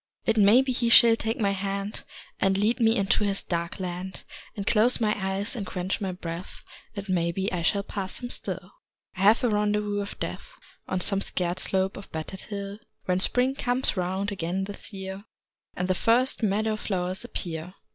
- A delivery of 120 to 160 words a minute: No, average, 190 wpm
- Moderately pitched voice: No, high, 200 Hz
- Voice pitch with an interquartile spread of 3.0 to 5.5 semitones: No, narrow, 2.5 semitones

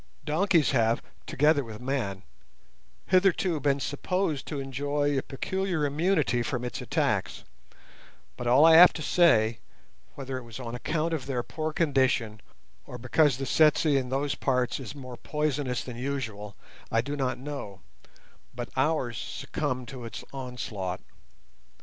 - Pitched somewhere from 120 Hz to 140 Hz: Yes, low, 135 Hz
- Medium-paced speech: Yes, average, 145 wpm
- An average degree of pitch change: Yes, average, 3.7 semitones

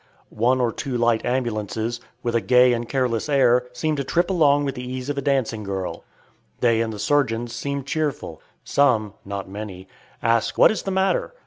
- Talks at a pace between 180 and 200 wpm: Yes, average, 190 wpm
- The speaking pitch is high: No, low, 125 Hz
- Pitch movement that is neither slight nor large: Yes, average, 3.8 semitones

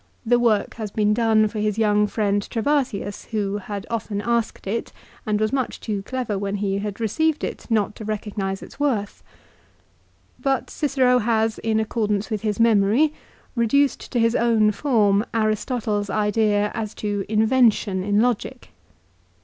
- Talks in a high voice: Yes, high, 215 Hz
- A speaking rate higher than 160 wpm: No, average, 155 wpm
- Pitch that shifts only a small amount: Yes, narrow, 2.2 semitones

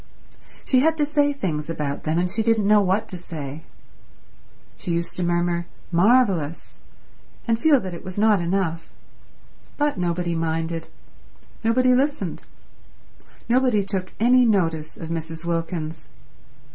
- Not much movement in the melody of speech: No, wide, 5.5 semitones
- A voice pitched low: No, medium, 180 Hz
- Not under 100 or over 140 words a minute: Yes, slow, 135 wpm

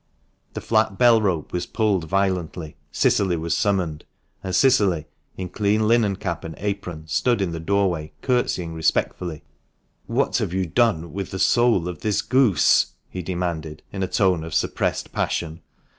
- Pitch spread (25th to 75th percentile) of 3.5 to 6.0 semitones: Yes, average, 3.8 semitones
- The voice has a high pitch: No, very low, 95 Hz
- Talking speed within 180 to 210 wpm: No, average, 165 wpm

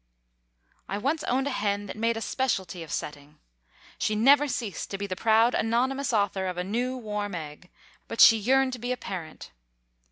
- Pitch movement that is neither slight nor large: Yes, average, 4.8 semitones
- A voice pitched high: Yes, high, 220 Hz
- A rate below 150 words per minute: No, average, 190 wpm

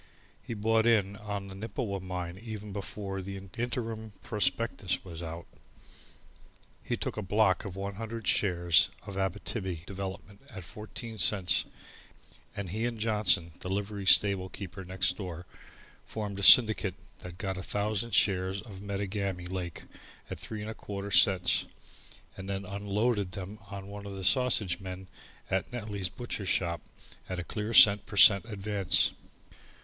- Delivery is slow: No, average, 145 wpm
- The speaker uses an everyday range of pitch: No, narrow, 2.2 semitones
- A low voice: Yes, low, 100 Hz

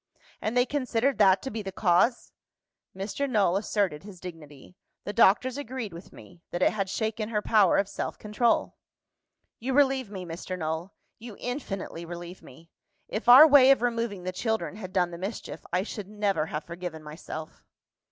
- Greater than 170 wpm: Yes, average, 180 wpm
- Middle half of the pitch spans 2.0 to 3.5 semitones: No, average, 4.6 semitones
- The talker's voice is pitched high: Yes, high, 200 Hz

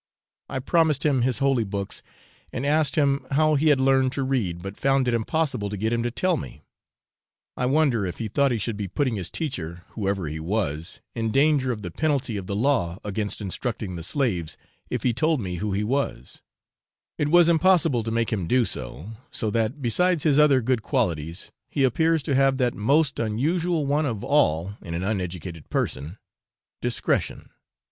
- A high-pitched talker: No, low, 120 Hz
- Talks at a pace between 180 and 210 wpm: Yes, average, 190 wpm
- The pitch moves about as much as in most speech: No, wide, 6.1 semitones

